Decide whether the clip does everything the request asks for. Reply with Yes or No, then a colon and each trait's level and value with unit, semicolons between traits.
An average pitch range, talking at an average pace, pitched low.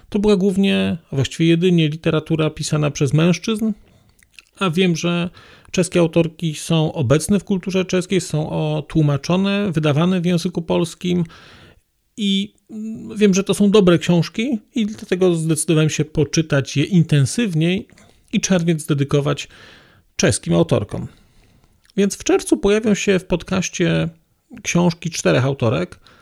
No: average, 4.1 semitones; average, 125 wpm; medium, 175 Hz